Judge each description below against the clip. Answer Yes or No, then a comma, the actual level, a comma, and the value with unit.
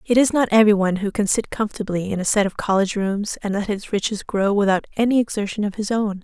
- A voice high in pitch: Yes, high, 205 Hz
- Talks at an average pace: No, fast, 250 wpm